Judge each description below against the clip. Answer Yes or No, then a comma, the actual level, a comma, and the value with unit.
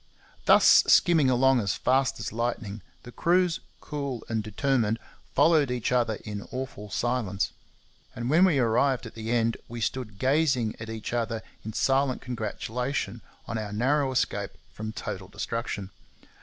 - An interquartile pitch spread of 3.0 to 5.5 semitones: Yes, average, 3.4 semitones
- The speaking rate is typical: Yes, average, 150 wpm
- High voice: No, low, 120 Hz